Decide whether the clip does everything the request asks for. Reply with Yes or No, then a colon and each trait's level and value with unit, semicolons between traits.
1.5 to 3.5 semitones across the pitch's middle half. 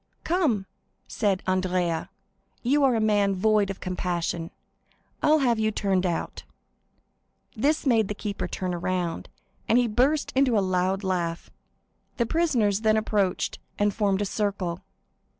No: average, 3.9 semitones